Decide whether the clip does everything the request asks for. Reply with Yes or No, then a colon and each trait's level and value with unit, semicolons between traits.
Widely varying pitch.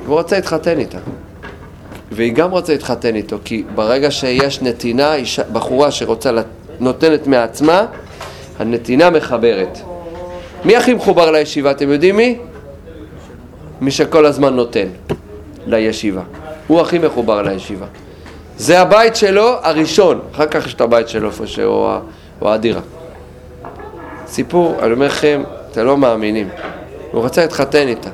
Yes: wide, 7.1 semitones